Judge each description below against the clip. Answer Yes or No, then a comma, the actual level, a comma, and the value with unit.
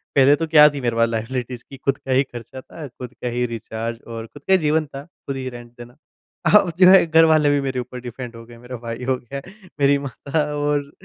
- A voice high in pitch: No, low, 130 Hz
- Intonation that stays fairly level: No, average, 3.3 semitones